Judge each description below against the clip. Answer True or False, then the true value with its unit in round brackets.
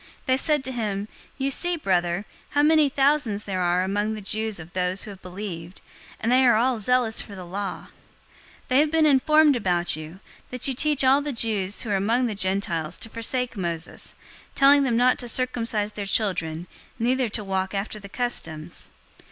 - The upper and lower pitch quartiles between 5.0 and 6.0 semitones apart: True (5.3 semitones)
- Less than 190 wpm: False (195 wpm)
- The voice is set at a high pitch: True (215 Hz)